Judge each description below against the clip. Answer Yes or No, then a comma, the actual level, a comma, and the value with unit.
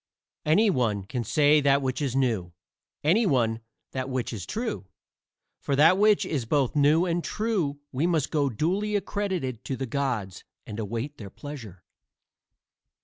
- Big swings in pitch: Yes, wide, 6.0 semitones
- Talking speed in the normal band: Yes, average, 155 wpm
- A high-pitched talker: No, medium, 140 Hz